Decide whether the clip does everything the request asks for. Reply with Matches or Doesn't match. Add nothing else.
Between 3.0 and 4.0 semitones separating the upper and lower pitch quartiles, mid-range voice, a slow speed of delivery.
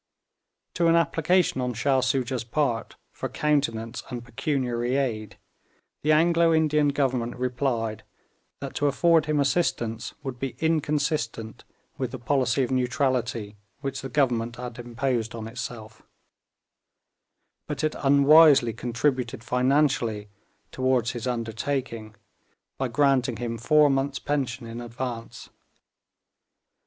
Doesn't match